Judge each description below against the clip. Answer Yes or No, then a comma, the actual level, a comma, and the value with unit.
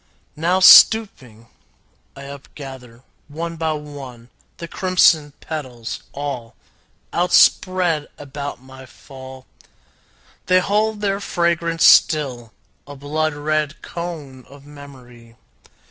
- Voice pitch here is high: No, medium, 145 Hz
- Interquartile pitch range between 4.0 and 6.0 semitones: Yes, average, 4.3 semitones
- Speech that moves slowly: Yes, slow, 100 wpm